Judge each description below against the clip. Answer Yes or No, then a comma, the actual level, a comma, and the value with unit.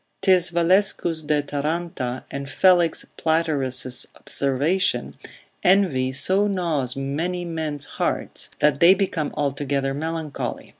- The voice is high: No, medium, 155 Hz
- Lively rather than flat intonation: No, average, 4.0 semitones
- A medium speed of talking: No, slow, 105 wpm